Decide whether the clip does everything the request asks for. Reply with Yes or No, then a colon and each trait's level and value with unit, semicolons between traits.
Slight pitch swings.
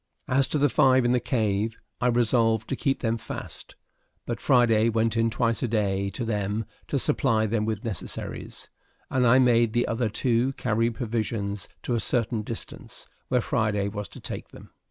Yes: narrow, 2.1 semitones